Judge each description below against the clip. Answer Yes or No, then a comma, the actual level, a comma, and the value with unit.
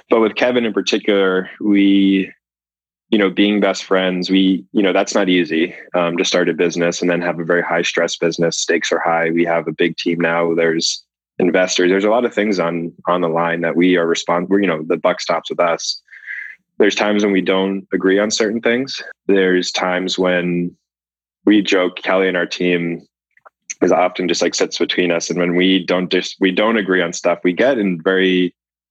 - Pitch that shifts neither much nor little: No, narrow, 2.1 semitones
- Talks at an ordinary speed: No, fast, 210 wpm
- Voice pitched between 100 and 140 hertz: No, very low, 90 Hz